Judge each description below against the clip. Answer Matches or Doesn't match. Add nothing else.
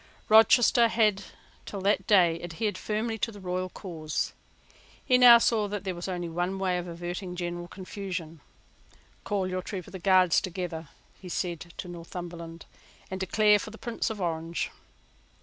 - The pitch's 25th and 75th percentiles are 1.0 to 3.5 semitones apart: Matches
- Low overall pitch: Doesn't match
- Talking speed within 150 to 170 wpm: Matches